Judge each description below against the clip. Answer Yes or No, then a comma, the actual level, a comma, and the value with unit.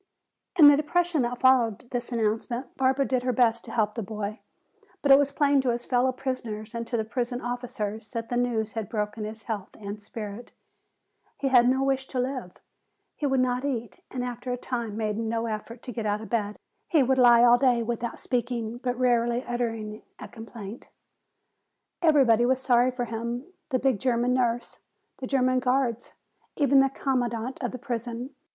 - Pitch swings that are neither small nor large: No, narrow, 2.3 semitones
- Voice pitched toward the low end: No, high, 245 Hz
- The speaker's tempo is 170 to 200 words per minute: Yes, average, 185 wpm